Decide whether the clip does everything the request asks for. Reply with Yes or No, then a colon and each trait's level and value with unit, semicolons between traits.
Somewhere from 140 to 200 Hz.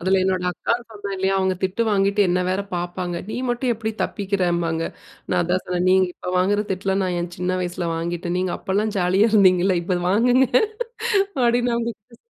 Yes: high, 190 Hz